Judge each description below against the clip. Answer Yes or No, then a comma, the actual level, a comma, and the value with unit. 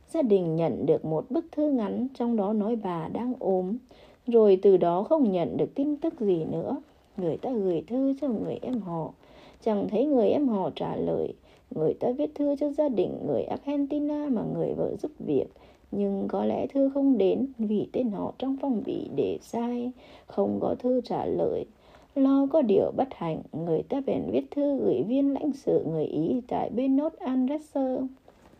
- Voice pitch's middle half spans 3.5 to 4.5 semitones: No, average, 5.2 semitones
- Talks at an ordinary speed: Yes, average, 190 wpm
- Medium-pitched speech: No, very high, 255 Hz